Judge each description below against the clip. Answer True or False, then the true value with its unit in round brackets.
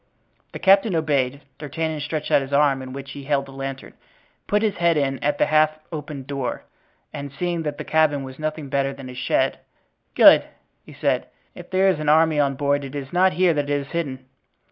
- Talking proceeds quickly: True (210 wpm)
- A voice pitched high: False (145 Hz)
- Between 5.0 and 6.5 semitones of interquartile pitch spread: False (2.6 semitones)